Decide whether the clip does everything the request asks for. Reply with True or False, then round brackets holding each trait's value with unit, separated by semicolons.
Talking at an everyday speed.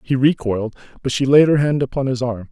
False (240 wpm)